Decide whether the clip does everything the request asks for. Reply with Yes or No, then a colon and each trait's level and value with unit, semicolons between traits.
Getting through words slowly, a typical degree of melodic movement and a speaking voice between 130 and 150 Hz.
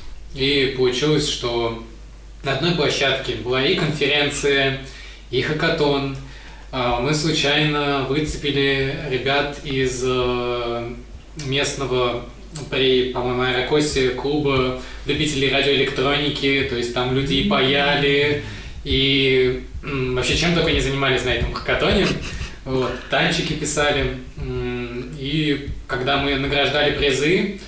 No: slow, 100 wpm; narrow, 2.1 semitones; low, 135 Hz